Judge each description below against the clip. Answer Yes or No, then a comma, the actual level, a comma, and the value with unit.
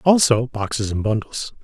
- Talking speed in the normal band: Yes, average, 145 wpm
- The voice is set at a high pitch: No, low, 120 Hz